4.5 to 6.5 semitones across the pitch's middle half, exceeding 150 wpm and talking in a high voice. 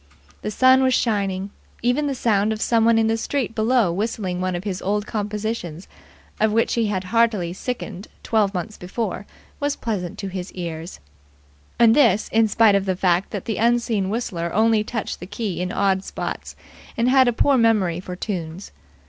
No: average, 3.6 semitones; average, 180 wpm; high, 210 Hz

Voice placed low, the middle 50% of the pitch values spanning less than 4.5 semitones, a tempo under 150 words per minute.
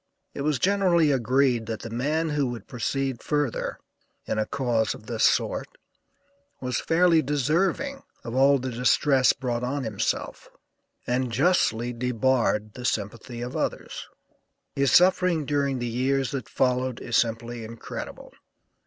Yes: low, 130 Hz; average, 3.6 semitones; average, 140 wpm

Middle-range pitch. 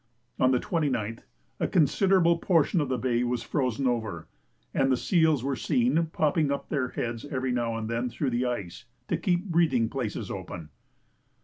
No: low, 130 Hz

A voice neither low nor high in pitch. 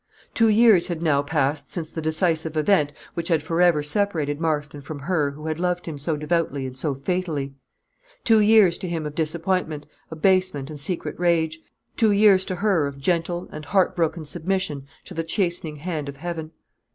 Yes: medium, 165 Hz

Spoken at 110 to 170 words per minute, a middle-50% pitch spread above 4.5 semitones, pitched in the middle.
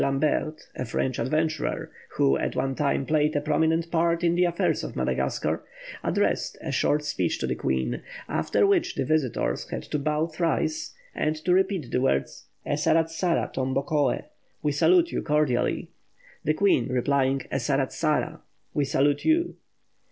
No: average, 150 wpm; average, 3.6 semitones; medium, 150 Hz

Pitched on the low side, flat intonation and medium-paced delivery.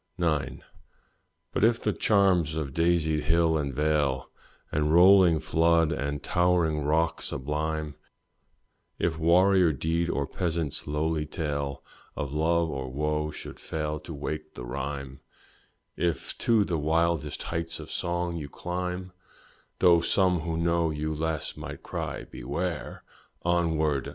No: very low, 80 Hz; narrow, 2.3 semitones; slow, 130 wpm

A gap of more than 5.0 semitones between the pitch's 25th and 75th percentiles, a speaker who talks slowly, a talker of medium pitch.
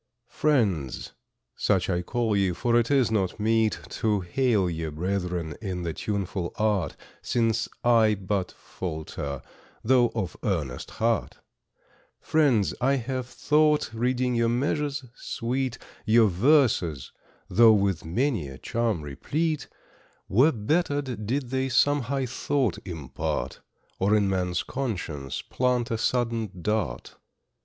No: wide, 5.6 semitones; slow, 125 wpm; low, 110 Hz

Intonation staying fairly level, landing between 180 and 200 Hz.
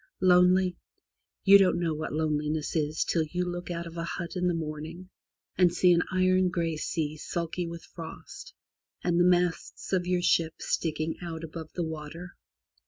No: narrow, 2.0 semitones; medium, 170 Hz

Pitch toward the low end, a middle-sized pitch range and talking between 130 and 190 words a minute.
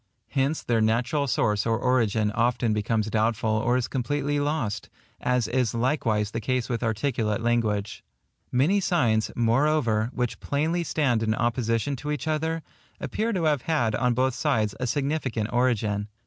Yes: low, 120 Hz; average, 4.4 semitones; average, 155 wpm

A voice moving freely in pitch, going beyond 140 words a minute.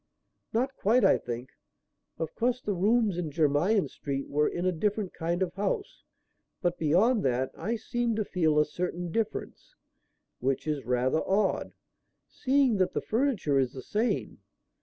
Yes: wide, 6.7 semitones; average, 160 wpm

